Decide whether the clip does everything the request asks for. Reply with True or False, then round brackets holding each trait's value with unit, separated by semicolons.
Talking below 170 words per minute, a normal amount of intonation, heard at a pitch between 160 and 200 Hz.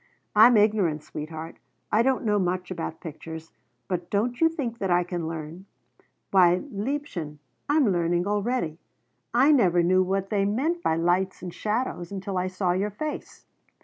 True (160 wpm; 4.1 semitones; 190 Hz)